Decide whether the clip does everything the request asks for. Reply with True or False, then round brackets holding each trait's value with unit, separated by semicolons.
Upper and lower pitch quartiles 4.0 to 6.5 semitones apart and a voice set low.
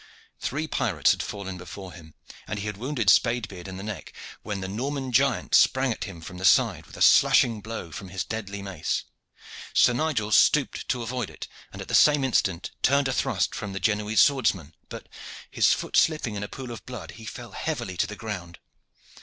True (4.8 semitones; 105 Hz)